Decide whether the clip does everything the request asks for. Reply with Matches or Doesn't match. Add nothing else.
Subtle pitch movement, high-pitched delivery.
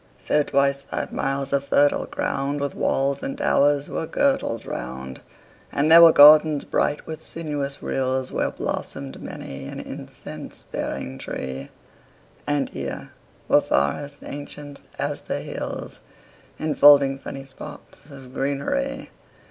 Doesn't match